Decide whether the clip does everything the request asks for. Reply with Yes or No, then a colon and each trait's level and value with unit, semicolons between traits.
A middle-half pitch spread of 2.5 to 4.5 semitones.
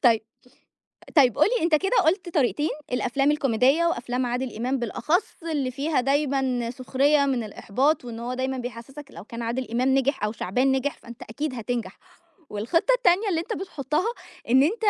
Yes: average, 3.9 semitones